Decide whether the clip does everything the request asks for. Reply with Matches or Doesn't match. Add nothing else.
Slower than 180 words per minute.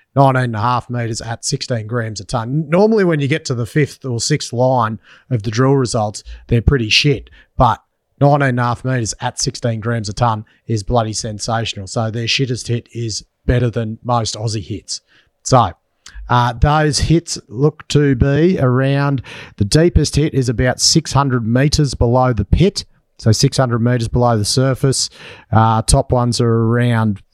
Matches